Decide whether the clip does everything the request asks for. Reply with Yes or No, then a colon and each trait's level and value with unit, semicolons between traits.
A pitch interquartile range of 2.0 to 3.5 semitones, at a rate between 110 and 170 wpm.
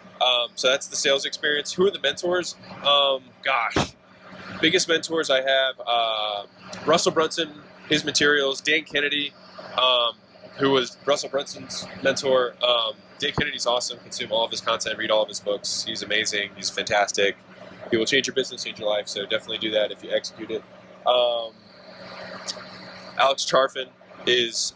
No: average, 4.4 semitones; average, 160 wpm